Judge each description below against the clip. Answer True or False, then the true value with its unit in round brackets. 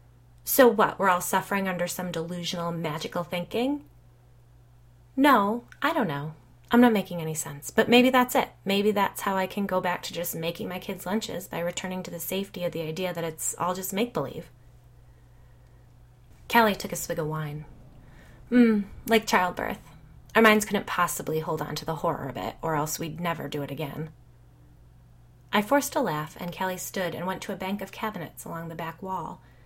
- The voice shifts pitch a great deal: True (5.9 semitones)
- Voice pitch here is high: False (175 Hz)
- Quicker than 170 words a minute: True (190 wpm)